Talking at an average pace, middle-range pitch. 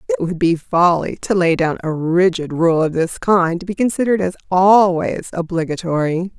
Yes: average, 180 wpm; medium, 175 Hz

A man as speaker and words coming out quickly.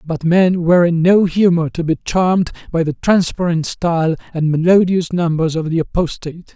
No: male; average, 175 wpm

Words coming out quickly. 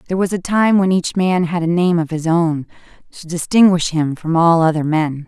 Yes: fast, 230 wpm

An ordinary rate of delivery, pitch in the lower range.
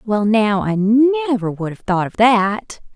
No: average, 185 wpm; high, 220 Hz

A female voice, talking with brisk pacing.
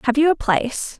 Yes: female; fast, 240 wpm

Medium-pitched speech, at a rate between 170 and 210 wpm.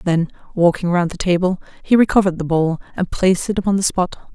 Yes: medium, 180 Hz; fast, 205 wpm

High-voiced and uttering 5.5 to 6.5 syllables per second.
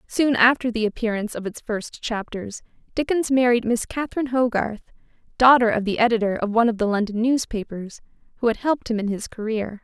Yes: high, 230 Hz; 6.0 syllables/s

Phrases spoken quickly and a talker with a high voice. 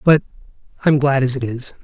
No: fast, 230 wpm; low, 135 Hz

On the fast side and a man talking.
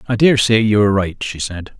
Yes: fast, 235 wpm; male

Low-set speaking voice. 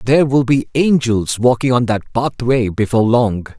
Yes: low, 120 Hz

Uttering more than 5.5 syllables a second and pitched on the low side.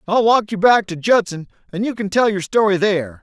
No: 5.7 syllables/s; high, 200 Hz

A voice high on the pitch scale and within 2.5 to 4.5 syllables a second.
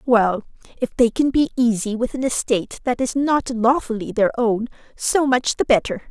No: high, 240 Hz; 4.8 syllables/s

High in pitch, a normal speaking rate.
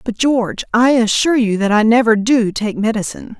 Yes: high, 225 Hz; average, 195 wpm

